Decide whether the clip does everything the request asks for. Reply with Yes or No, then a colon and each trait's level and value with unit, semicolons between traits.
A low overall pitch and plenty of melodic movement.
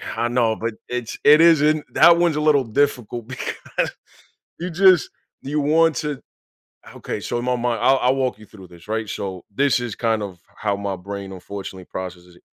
Yes: low, 120 Hz; wide, 6.6 semitones